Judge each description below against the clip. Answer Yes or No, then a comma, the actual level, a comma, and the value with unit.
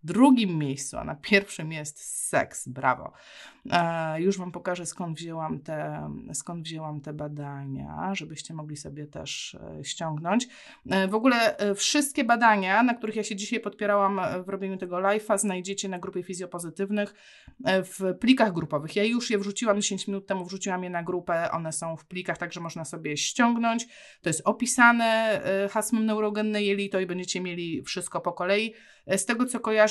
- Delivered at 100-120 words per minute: No, fast, 160 wpm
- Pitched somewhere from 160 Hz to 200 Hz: Yes, high, 190 Hz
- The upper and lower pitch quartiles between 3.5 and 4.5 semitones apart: Yes, average, 4.2 semitones